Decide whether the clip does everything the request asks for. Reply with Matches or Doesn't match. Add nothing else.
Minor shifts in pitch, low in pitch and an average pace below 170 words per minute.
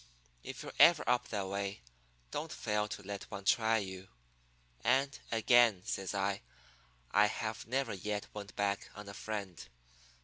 Matches